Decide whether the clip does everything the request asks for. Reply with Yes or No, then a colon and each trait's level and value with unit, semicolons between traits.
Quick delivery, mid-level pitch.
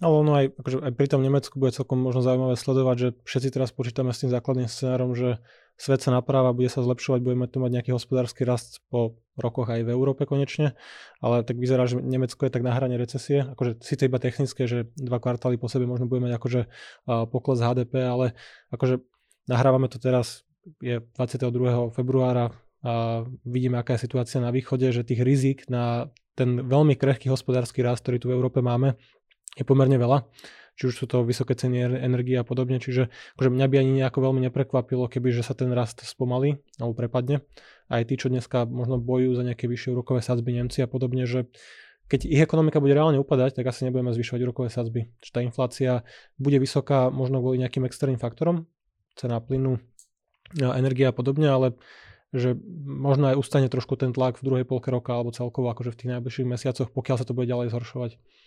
No: fast, 195 wpm; low, 125 Hz